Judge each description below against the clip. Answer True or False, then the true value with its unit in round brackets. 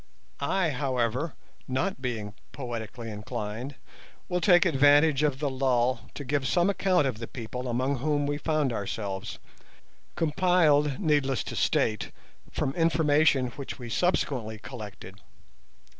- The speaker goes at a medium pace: False (130 wpm)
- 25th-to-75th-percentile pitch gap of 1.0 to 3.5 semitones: False (4.2 semitones)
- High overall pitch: False (135 Hz)